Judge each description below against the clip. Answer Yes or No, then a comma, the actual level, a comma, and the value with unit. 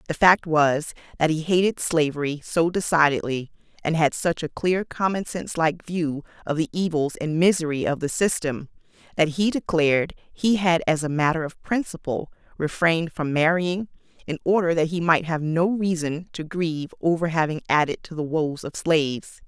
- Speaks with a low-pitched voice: No, medium, 165 Hz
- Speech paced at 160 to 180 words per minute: Yes, average, 175 wpm